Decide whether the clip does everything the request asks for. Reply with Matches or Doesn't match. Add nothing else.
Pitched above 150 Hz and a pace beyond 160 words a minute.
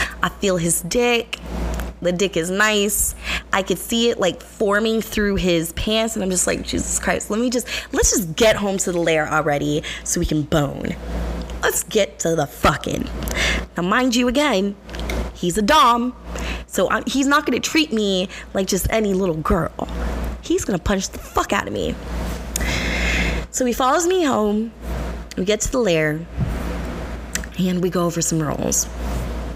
Matches